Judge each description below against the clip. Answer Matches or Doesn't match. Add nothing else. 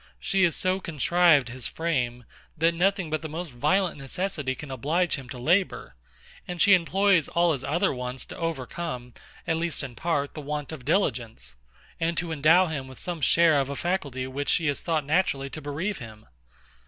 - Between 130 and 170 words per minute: Doesn't match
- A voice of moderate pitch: Matches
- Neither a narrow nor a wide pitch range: Matches